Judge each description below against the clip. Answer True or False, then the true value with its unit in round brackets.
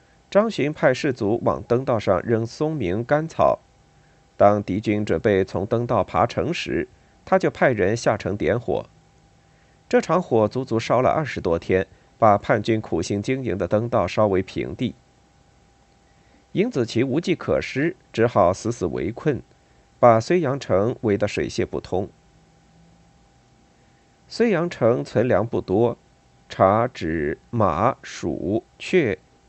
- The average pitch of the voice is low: True (110 Hz)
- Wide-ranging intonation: True (5.8 semitones)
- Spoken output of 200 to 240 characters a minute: False (190 characters per minute)